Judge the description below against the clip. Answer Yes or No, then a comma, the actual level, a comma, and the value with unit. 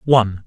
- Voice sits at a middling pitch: No, low, 115 Hz